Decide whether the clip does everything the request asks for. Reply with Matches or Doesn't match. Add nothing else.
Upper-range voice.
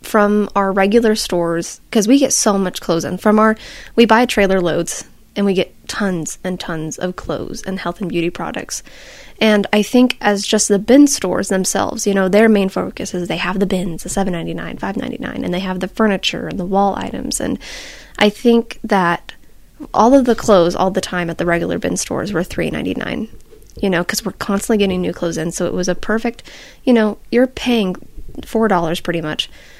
Matches